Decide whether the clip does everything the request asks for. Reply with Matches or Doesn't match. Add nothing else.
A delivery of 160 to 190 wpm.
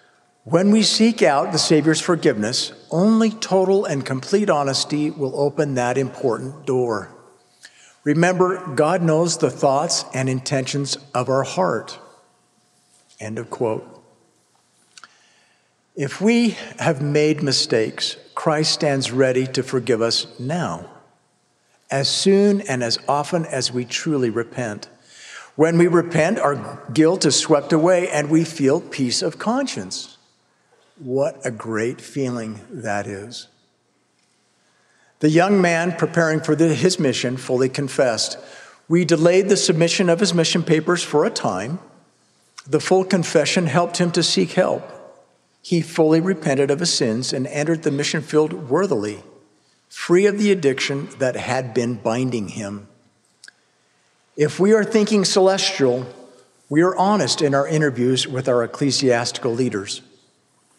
Doesn't match